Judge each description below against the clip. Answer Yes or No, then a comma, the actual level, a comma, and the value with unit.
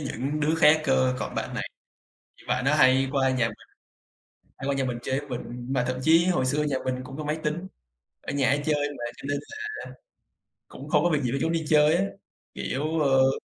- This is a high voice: No, medium, 140 Hz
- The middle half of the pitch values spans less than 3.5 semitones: Yes, average, 2.8 semitones